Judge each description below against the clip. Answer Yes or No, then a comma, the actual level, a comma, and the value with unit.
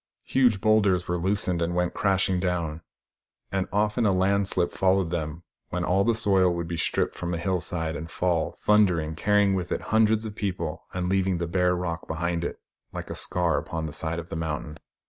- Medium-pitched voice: No, very low, 90 Hz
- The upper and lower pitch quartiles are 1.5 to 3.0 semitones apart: Yes, average, 2.7 semitones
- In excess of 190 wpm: Yes, average, 200 wpm